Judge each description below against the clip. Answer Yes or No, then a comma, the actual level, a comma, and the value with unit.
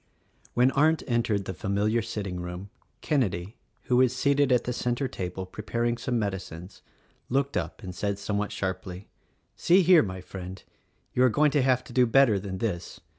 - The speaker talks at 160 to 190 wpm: Yes, average, 180 wpm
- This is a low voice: Yes, low, 110 Hz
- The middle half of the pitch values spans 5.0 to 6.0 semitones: Yes, average, 5.3 semitones